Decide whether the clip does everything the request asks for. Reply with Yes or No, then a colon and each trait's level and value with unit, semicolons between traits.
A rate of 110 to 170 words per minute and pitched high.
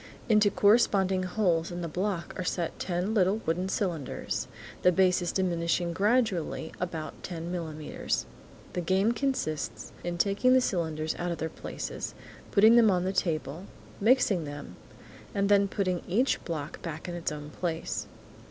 No: average, 150 wpm; medium, 180 Hz